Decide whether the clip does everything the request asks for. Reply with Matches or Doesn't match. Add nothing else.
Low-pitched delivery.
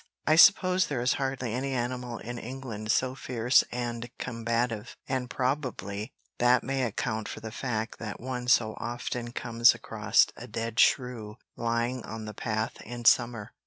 Matches